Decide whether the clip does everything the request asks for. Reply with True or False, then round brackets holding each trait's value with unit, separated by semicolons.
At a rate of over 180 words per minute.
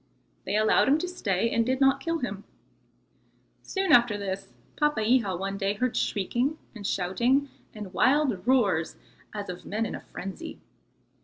False (155 wpm)